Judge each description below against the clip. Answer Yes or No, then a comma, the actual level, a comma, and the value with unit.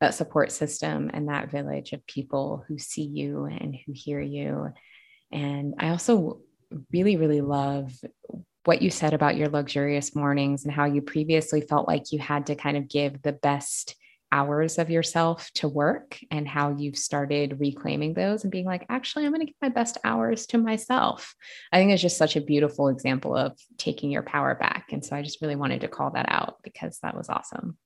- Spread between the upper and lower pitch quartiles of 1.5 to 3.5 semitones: Yes, narrow, 2.6 semitones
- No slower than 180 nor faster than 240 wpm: Yes, average, 200 wpm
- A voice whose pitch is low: No, medium, 145 Hz